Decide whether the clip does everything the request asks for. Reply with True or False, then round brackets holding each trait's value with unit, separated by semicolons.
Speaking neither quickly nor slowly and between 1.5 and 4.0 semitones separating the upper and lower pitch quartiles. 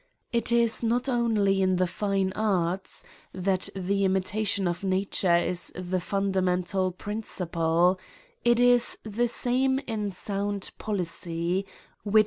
False (115 wpm; 3.3 semitones)